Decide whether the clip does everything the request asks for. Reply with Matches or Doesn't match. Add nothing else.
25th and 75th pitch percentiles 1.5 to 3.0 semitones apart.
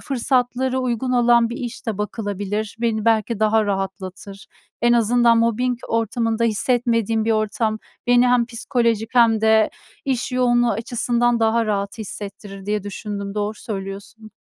Matches